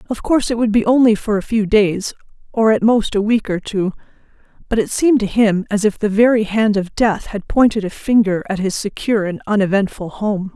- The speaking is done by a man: No, female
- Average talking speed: No, fast, 220 wpm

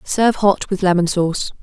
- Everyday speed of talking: Yes, average, 185 wpm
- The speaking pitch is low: No, high, 190 Hz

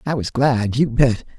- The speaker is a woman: No, male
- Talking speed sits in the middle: No, fast, 215 wpm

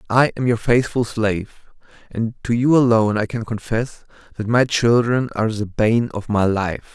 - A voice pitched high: No, low, 115 Hz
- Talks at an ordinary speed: Yes, average, 180 wpm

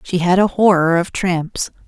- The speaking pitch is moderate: Yes, medium, 180 Hz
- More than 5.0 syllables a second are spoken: No, 4.3 syllables/s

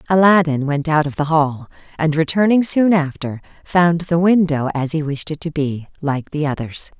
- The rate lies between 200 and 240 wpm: No, average, 190 wpm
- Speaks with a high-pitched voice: No, medium, 155 Hz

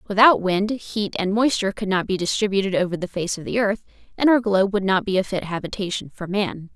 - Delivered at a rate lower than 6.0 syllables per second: No, 6.2 syllables/s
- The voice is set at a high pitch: Yes, high, 200 Hz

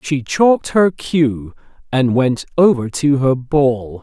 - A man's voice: Yes, male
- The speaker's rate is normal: Yes, average, 150 wpm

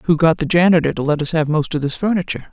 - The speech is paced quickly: Yes, fast, 285 wpm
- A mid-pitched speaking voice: Yes, medium, 160 Hz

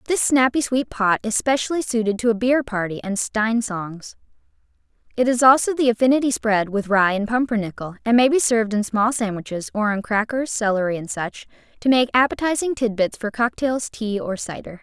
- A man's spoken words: No, female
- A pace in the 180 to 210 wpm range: Yes, average, 185 wpm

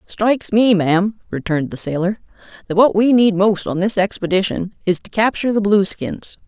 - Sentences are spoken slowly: No, average, 175 wpm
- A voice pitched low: No, high, 200 Hz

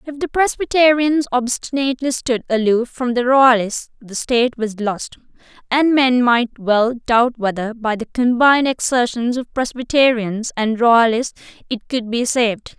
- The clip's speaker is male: No, female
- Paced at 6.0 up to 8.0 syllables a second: No, 4.4 syllables/s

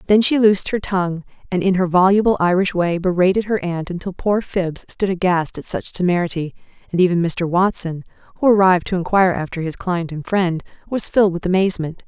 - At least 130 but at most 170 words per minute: No, average, 195 wpm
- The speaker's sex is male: No, female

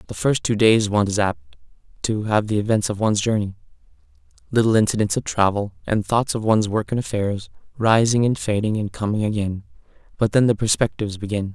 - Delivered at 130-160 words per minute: No, average, 185 wpm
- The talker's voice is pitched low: Yes, low, 105 Hz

